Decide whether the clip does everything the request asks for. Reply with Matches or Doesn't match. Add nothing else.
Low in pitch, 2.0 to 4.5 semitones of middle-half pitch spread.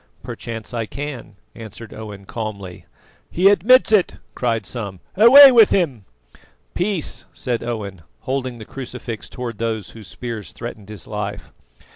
Doesn't match